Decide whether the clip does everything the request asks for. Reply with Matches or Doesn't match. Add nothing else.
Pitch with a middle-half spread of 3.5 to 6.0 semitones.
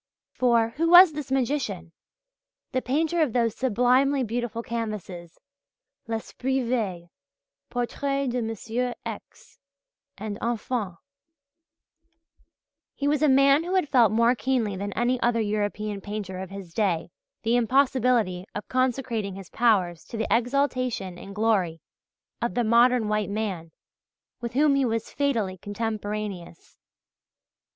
Matches